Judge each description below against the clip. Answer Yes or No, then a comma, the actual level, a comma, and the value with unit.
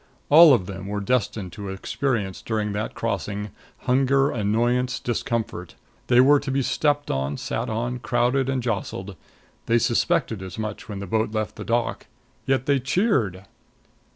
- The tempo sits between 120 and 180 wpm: Yes, average, 155 wpm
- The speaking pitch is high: No, low, 115 Hz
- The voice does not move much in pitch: No, average, 4.3 semitones